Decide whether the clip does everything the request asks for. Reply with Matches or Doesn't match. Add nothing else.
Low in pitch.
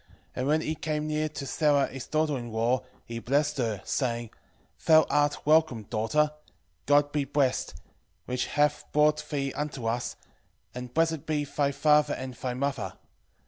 Doesn't match